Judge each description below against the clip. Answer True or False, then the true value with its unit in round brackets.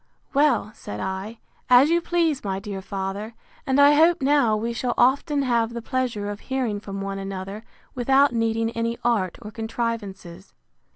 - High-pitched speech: True (230 Hz)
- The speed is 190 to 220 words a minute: False (165 wpm)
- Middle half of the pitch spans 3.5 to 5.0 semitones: True (4.7 semitones)